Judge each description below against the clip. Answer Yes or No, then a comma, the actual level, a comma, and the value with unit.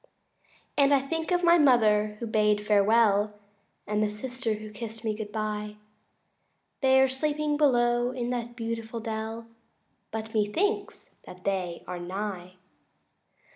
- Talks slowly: No, average, 150 wpm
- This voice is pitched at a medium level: No, high, 225 Hz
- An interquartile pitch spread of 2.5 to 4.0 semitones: Yes, average, 3.5 semitones